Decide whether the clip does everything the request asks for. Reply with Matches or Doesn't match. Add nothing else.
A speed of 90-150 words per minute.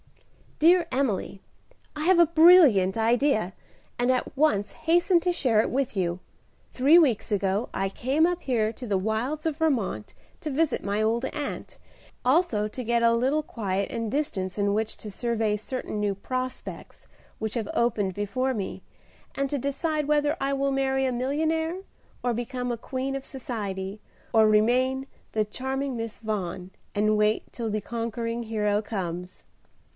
Doesn't match